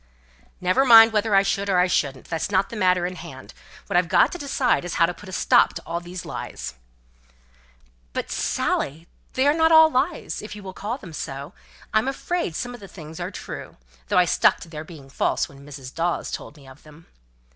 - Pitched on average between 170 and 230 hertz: Yes, medium, 185 Hz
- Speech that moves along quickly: Yes, fast, 210 wpm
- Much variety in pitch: Yes, wide, 6.0 semitones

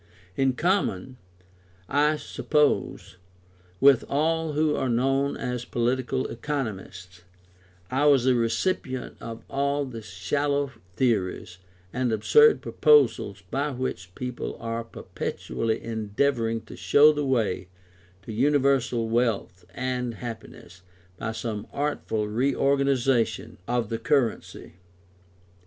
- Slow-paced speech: Yes, slow, 110 wpm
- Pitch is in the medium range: No, low, 125 Hz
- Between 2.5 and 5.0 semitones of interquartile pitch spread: Yes, average, 3.8 semitones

